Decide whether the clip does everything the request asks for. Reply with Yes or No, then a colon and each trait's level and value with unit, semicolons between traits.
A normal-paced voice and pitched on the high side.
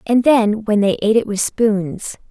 No: fast, 210 wpm; high, 215 Hz